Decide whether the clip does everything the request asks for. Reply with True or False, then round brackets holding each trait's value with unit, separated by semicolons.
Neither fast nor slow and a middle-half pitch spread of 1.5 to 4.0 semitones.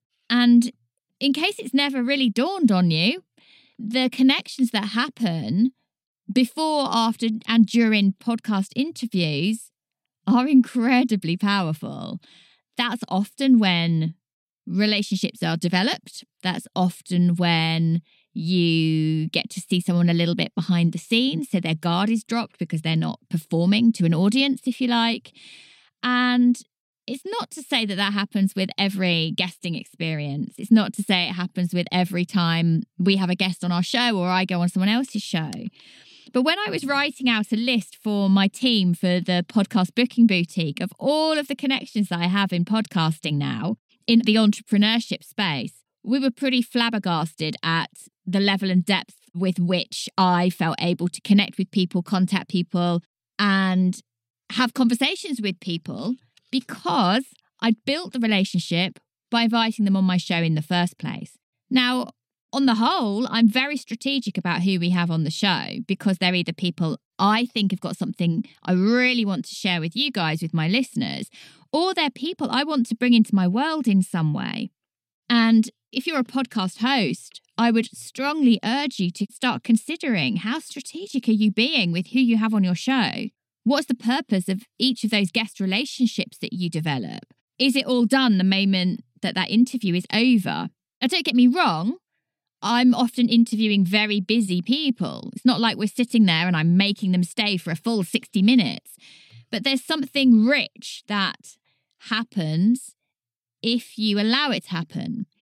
False (170 wpm; 5.1 semitones)